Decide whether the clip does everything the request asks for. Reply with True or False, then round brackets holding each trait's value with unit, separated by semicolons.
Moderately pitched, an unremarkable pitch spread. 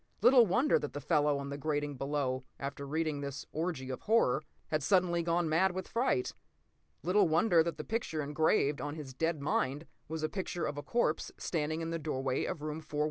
True (155 Hz; 3.2 semitones)